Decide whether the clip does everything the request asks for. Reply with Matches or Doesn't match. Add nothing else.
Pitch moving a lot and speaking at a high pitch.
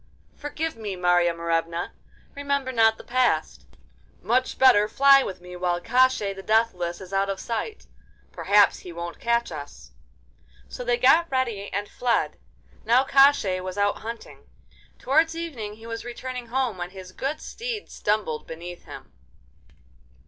Matches